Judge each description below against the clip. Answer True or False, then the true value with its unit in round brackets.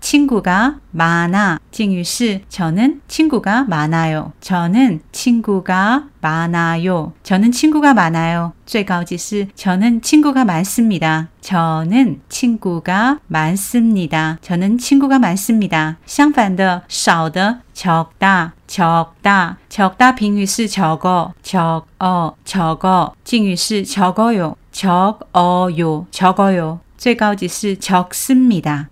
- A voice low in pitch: False (190 Hz)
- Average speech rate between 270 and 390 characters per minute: False (195 characters per minute)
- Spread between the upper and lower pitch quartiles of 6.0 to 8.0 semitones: False (5.1 semitones)